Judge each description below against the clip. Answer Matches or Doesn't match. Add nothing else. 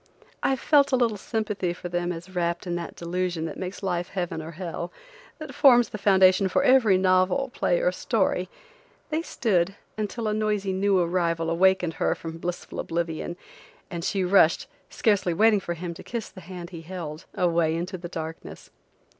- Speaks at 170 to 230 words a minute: Matches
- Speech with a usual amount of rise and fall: Matches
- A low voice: Doesn't match